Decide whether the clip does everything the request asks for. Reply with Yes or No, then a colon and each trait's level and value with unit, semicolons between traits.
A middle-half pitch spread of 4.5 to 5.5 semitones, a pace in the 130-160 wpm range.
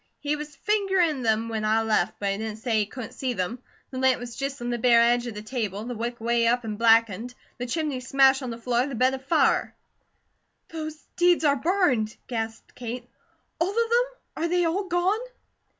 No: average, 5.0 semitones; fast, 205 wpm